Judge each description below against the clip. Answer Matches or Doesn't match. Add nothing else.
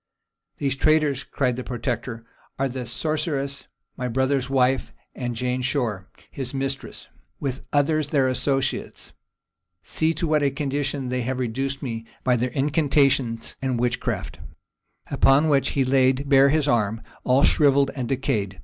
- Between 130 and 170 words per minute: Matches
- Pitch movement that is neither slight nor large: Doesn't match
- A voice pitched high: Doesn't match